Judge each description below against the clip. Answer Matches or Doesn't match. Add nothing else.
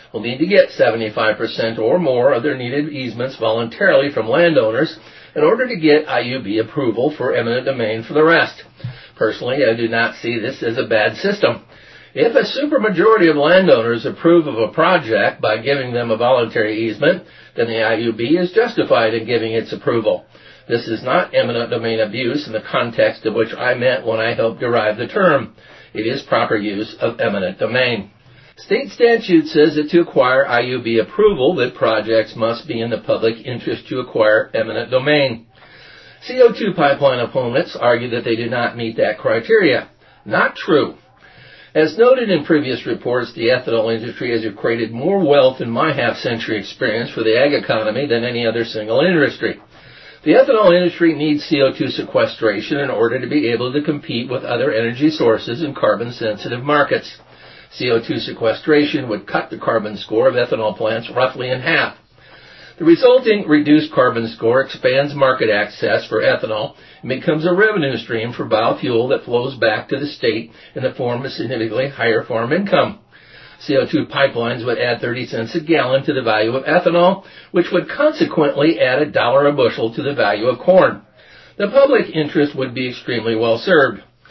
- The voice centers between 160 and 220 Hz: Doesn't match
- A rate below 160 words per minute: Doesn't match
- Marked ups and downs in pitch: Matches